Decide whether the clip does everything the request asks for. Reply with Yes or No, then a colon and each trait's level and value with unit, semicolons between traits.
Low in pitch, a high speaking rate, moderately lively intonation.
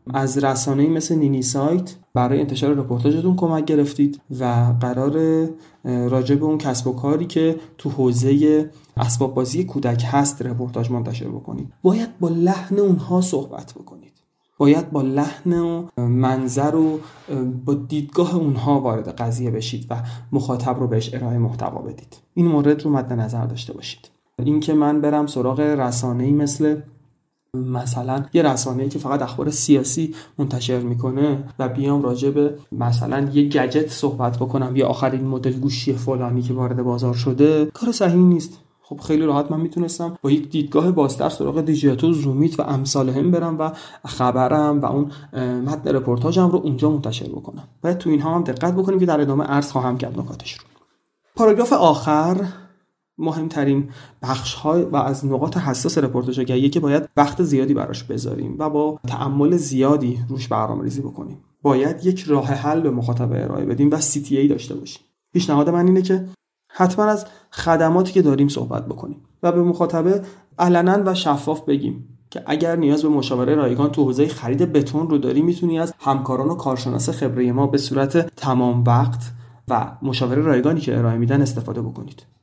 No: medium, 145 Hz; fast, 165 wpm; average, 3.6 semitones